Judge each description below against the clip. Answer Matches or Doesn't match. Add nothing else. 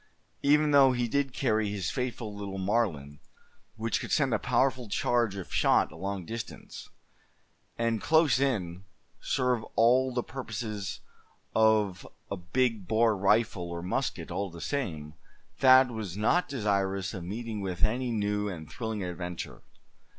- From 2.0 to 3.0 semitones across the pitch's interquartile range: Doesn't match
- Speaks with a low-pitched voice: Matches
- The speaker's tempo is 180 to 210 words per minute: Doesn't match